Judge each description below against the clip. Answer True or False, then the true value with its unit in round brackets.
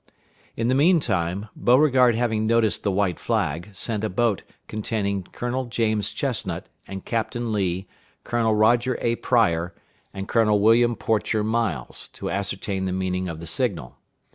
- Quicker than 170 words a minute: False (150 wpm)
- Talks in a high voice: False (110 Hz)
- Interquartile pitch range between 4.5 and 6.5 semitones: False (3.6 semitones)